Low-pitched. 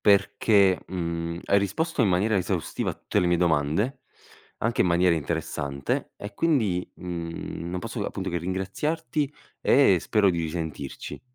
Yes: very low, 90 Hz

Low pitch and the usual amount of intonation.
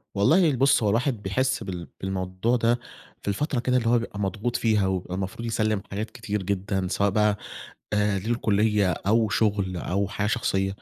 Yes: low, 105 Hz; average, 3.2 semitones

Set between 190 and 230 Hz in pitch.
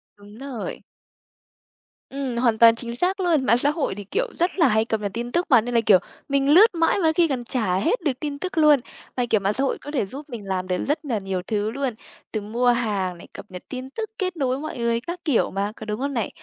No: high, 245 Hz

